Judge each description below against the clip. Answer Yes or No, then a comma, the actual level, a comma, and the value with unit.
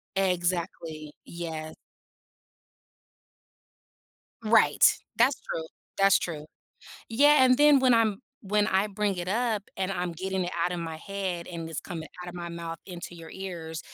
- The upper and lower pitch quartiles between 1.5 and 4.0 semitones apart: Yes, average, 3.6 semitones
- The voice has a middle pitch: Yes, medium, 180 Hz